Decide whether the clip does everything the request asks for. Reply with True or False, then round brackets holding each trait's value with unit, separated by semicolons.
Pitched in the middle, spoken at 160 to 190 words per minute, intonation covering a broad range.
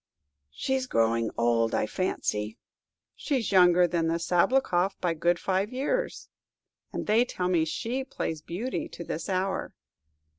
False (180 Hz; 140 wpm; 6.1 semitones)